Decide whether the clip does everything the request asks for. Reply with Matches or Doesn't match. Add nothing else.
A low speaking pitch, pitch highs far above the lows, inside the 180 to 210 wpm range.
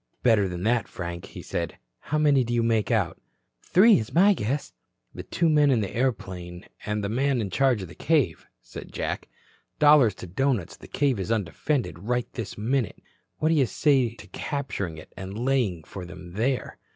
Matches